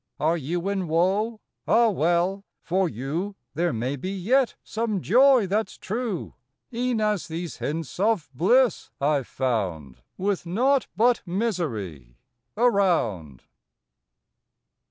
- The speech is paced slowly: Yes, slow, 130 wpm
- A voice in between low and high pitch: Yes, medium, 180 Hz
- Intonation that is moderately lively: No, wide, 6.7 semitones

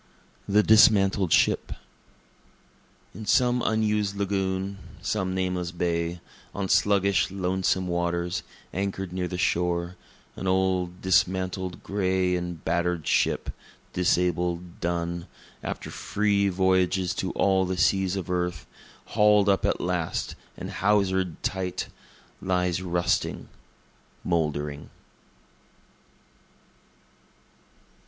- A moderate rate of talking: No, slow, 100 wpm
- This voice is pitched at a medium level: No, very low, 95 Hz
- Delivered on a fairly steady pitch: Yes, narrow, 1.8 semitones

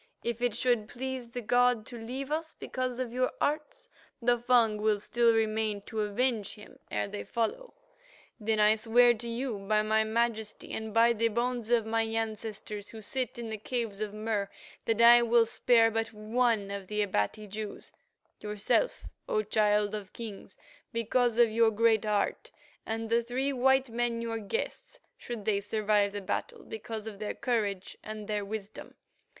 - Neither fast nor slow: Yes, average, 175 wpm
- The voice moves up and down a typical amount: No, narrow, 2.2 semitones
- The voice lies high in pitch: Yes, high, 225 Hz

